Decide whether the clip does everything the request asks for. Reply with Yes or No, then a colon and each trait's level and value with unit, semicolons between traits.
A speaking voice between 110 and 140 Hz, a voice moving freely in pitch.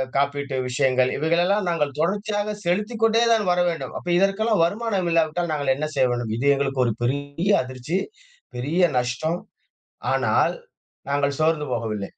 No: medium, 155 Hz; wide, 5.9 semitones